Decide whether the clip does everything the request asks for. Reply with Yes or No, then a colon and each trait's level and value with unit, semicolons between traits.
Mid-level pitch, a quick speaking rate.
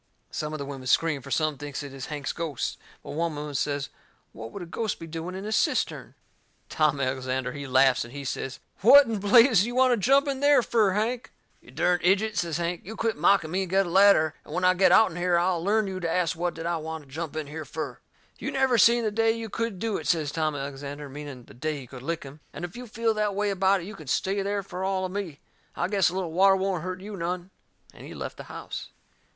Yes: medium, 175 Hz; fast, 255 wpm